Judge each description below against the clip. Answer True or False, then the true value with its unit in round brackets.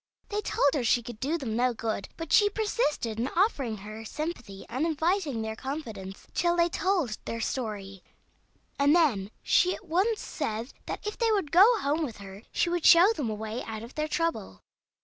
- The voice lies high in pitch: True (280 Hz)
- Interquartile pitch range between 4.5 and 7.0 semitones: False (7.6 semitones)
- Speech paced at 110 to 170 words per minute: False (195 wpm)